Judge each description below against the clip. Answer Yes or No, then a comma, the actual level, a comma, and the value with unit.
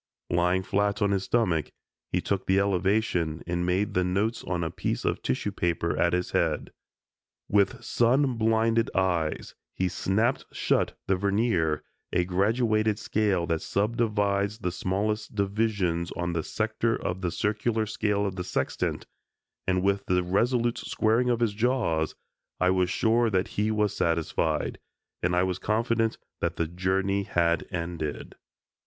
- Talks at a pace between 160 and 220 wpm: No, average, 150 wpm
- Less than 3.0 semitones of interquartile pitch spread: No, average, 3.5 semitones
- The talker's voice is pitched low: Yes, low, 100 Hz